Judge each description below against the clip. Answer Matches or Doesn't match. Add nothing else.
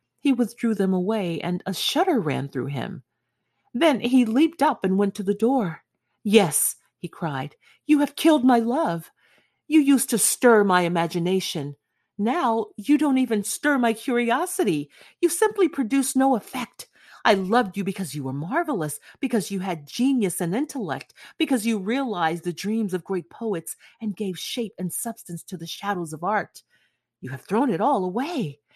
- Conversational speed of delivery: Matches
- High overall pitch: Matches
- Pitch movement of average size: Doesn't match